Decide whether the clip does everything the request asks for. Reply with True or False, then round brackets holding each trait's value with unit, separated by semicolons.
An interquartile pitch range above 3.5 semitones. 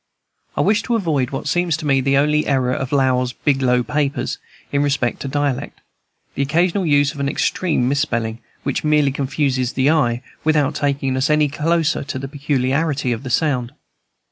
False (2.6 semitones)